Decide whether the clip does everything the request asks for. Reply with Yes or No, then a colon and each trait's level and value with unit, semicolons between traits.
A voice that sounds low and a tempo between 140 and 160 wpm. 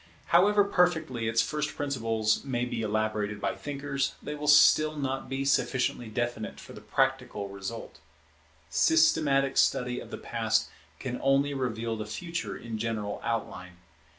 Yes: low, 125 Hz; average, 145 wpm